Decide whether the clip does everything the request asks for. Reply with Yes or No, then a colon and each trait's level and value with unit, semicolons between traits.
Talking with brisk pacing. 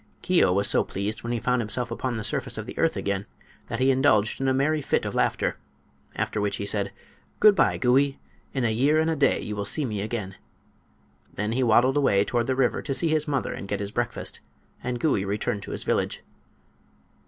Yes: fast, 220 wpm